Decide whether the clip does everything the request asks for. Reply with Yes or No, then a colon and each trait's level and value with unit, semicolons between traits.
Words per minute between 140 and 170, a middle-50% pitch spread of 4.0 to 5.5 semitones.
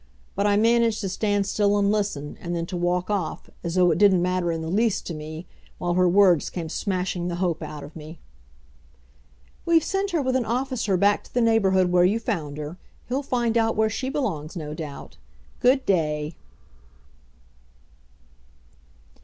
No: average, 180 wpm; average, 4.7 semitones